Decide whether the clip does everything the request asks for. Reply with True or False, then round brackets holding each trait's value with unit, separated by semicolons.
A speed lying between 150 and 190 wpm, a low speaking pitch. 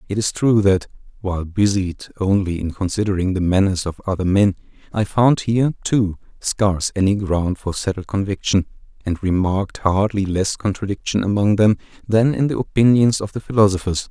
True (160 wpm; 100 Hz)